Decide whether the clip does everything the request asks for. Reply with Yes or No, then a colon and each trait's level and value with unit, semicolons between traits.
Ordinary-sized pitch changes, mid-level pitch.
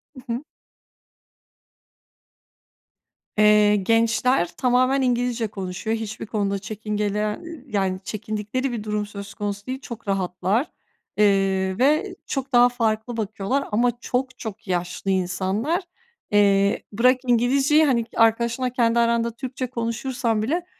No: average, 3.5 semitones; high, 225 Hz